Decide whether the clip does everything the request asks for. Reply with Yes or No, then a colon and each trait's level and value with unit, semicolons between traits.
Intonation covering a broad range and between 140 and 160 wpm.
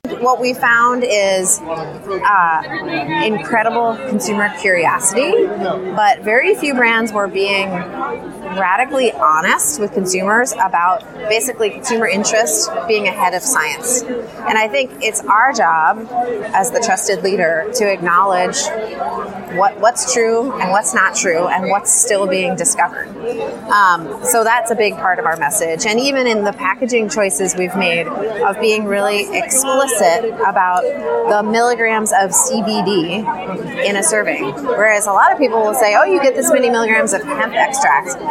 No: average, 3.6 semitones; average, 150 wpm